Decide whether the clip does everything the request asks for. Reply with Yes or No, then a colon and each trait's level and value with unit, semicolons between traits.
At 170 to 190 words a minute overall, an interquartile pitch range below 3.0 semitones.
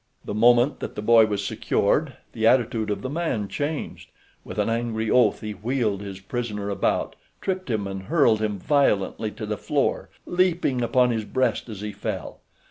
No: average, 180 wpm; average, 3.5 semitones